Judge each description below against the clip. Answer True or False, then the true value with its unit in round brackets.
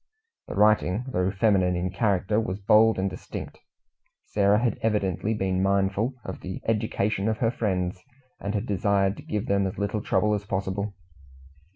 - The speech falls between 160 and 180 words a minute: True (165 wpm)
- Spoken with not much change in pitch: True (2.0 semitones)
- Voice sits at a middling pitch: False (100 Hz)